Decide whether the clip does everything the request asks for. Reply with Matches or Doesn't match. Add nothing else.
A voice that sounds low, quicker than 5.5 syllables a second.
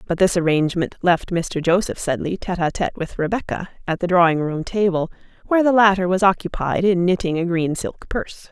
Doesn't match